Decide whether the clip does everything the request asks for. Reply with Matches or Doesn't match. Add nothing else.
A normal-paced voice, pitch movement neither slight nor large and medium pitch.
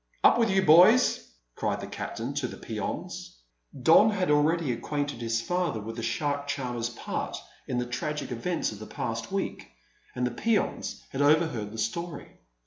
Doesn't match